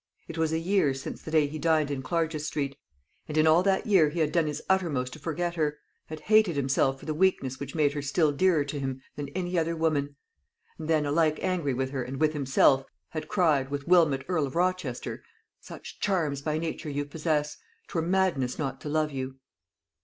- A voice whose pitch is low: No, medium, 155 Hz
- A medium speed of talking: No, fast, 210 wpm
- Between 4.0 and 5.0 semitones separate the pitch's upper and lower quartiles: No, average, 2.9 semitones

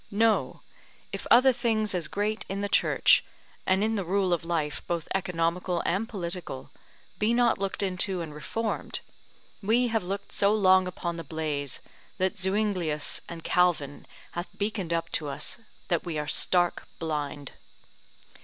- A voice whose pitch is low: No, medium, 180 Hz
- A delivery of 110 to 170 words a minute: Yes, average, 155 wpm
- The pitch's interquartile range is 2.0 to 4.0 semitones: Yes, average, 3.6 semitones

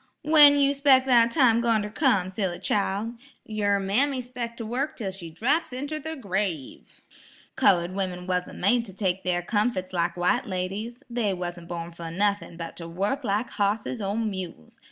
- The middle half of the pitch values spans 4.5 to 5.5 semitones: Yes, average, 5.0 semitones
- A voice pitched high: Yes, high, 205 Hz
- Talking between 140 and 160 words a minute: No, average, 175 wpm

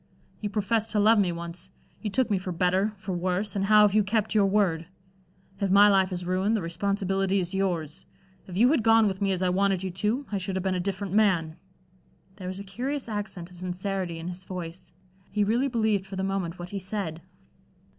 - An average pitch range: No, narrow, 2.3 semitones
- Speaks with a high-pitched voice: Yes, high, 195 Hz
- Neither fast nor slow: No, fast, 220 wpm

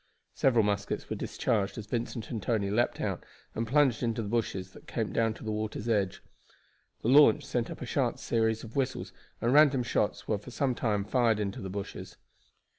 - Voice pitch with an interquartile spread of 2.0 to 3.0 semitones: Yes, narrow, 2.6 semitones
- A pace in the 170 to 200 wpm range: Yes, average, 195 wpm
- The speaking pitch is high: No, low, 110 Hz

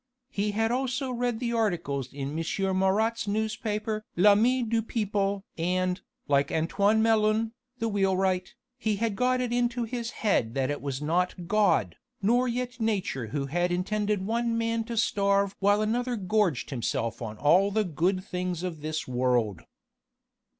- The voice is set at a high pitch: Yes, high, 200 Hz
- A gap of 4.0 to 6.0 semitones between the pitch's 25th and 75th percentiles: Yes, average, 4.6 semitones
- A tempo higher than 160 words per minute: No, average, 155 wpm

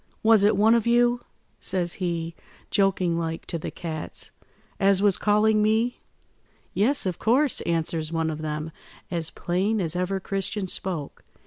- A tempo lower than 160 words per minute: Yes, average, 150 wpm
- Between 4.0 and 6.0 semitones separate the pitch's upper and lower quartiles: Yes, average, 4.3 semitones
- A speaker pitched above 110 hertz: Yes, high, 190 Hz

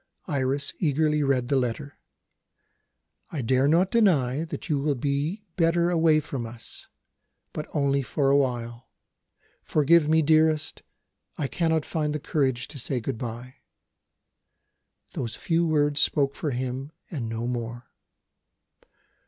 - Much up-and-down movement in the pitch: No, average, 3.6 semitones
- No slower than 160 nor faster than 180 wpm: No, slow, 135 wpm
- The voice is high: No, medium, 140 Hz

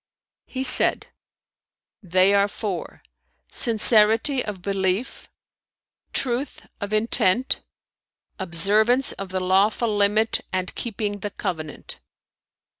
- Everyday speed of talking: No, slow, 100 wpm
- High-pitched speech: Yes, high, 205 Hz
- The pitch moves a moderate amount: Yes, average, 3.1 semitones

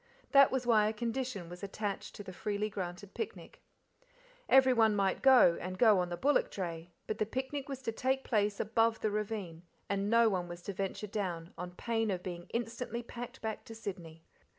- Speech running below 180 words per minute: No, average, 195 wpm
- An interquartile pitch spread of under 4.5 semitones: Yes, average, 4.1 semitones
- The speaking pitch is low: No, high, 210 Hz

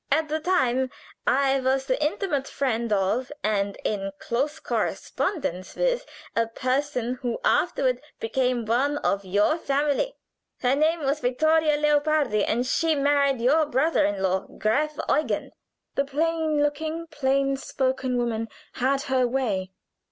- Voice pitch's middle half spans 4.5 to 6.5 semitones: No, average, 3.9 semitones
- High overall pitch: Yes, very high, 275 Hz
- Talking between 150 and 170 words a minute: No, slow, 135 wpm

